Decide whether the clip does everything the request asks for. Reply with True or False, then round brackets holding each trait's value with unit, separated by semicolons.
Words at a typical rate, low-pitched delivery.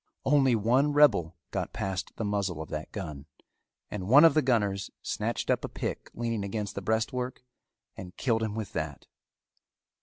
True (170 wpm; 105 Hz)